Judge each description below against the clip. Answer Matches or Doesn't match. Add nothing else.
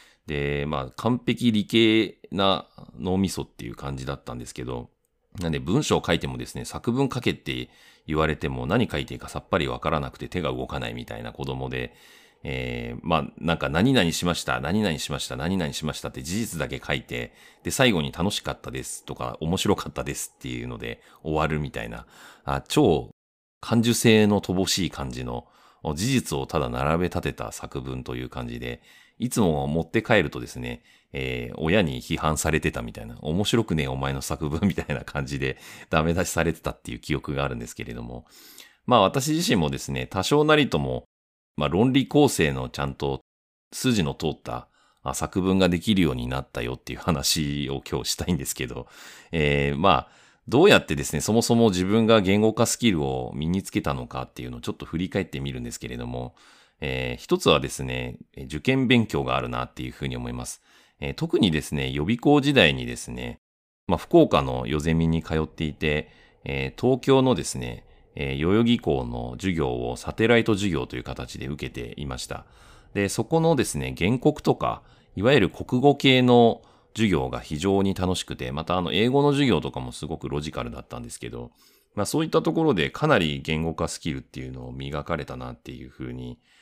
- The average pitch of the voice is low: Matches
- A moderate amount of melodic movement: Doesn't match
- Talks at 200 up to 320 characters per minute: Doesn't match